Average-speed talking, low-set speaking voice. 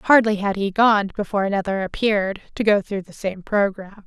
No: average, 190 wpm; high, 200 Hz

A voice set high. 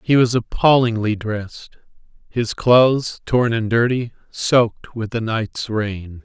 No: low, 115 Hz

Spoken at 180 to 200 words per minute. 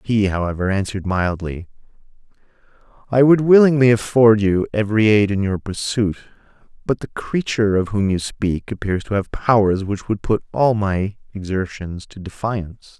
No: average, 150 wpm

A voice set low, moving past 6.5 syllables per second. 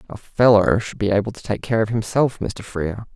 No: low, 110 Hz; 5.5 syllables/s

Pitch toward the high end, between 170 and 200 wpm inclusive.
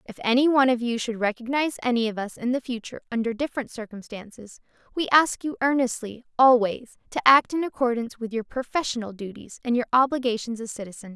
Yes: high, 240 Hz; average, 185 wpm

